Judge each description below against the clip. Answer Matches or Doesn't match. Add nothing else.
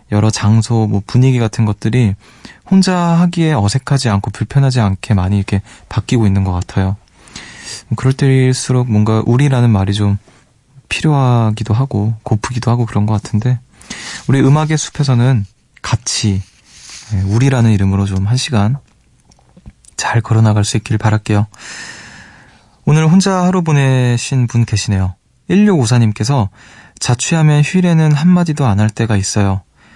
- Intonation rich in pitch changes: Doesn't match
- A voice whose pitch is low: Matches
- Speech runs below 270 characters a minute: Doesn't match